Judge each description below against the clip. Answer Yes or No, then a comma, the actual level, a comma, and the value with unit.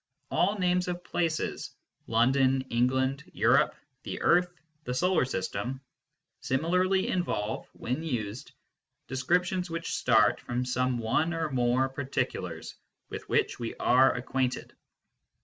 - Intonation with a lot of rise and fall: Yes, wide, 5.7 semitones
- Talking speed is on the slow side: Yes, slow, 115 wpm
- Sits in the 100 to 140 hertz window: Yes, low, 135 Hz